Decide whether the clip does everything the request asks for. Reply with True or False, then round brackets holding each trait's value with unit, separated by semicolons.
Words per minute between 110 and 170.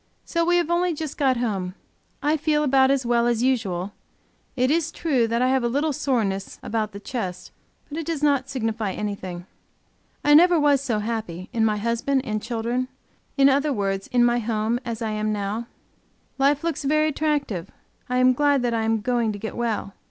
False (195 wpm)